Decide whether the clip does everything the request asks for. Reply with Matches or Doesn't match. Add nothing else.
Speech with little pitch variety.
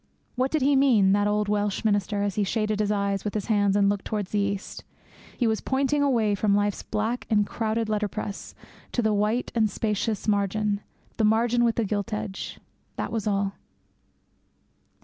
Matches